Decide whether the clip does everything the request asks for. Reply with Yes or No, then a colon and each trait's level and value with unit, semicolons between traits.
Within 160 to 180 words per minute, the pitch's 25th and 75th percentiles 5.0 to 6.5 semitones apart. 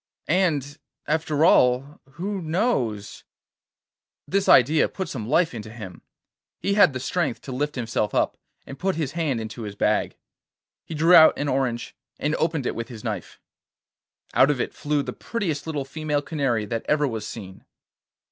Yes: average, 165 wpm; wide, 5.4 semitones